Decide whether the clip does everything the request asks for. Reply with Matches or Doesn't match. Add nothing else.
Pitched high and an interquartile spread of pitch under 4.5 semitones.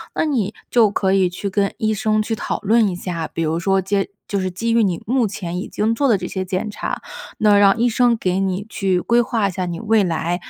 Matches